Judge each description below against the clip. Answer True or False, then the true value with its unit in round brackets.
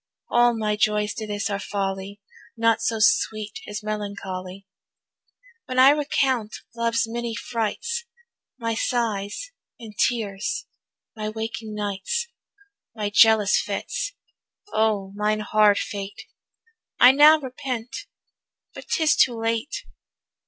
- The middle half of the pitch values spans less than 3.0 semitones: True (2.5 semitones)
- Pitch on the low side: False (220 Hz)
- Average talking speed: False (115 wpm)